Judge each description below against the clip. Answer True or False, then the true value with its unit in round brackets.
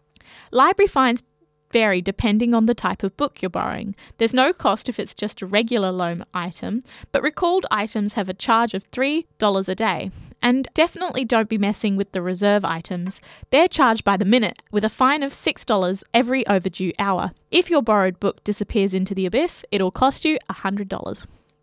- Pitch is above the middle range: True (210 Hz)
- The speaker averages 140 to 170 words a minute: False (190 wpm)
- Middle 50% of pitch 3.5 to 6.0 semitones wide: True (4.7 semitones)